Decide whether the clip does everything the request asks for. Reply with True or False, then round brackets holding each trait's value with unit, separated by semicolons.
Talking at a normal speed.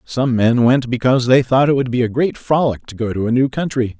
False (270 wpm)